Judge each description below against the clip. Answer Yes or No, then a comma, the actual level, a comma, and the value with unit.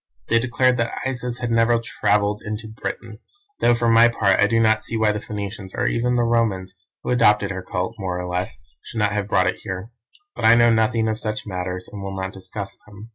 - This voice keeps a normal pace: No, fast, 225 wpm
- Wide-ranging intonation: No, average, 3.0 semitones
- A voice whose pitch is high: No, low, 110 Hz